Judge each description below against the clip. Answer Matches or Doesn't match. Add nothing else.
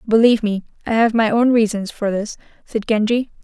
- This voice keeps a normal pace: Matches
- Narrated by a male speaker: Doesn't match